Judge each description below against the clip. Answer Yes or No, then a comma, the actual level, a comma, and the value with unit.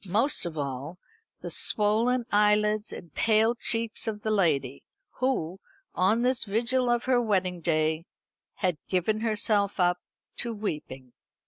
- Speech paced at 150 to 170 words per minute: No, slow, 135 wpm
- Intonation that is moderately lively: Yes, average, 4.7 semitones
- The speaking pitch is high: Yes, high, 210 Hz